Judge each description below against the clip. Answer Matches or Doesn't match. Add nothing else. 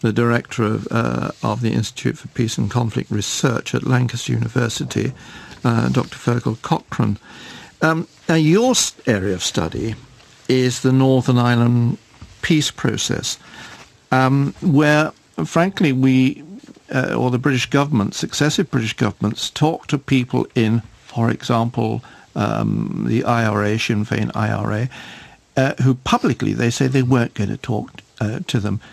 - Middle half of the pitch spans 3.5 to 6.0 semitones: Doesn't match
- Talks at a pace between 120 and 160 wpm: Matches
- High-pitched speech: Doesn't match